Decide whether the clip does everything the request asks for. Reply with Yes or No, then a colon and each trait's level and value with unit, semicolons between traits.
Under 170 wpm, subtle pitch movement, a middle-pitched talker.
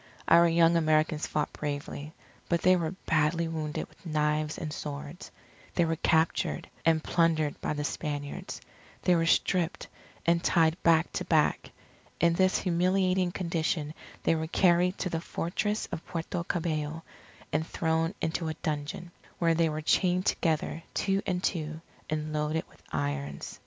Yes: average, 150 wpm; narrow, 2.1 semitones; medium, 165 Hz